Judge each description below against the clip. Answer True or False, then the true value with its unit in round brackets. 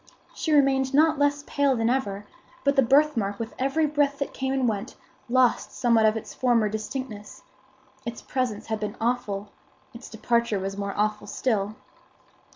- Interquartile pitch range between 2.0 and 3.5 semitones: False (4.1 semitones)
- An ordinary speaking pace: True (160 wpm)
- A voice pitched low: False (235 Hz)